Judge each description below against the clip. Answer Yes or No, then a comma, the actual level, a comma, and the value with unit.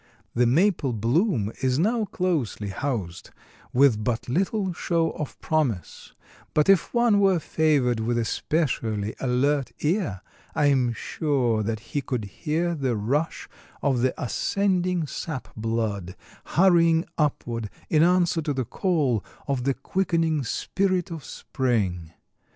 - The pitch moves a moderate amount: No, wide, 6.4 semitones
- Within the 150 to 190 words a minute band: No, slow, 135 wpm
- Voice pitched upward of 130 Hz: Yes, medium, 140 Hz